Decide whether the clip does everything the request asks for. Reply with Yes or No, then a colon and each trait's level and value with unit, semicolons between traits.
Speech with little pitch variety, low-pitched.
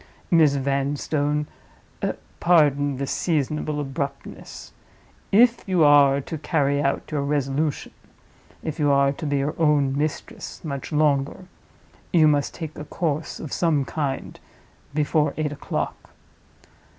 No: narrow, 1.9 semitones; medium, 145 Hz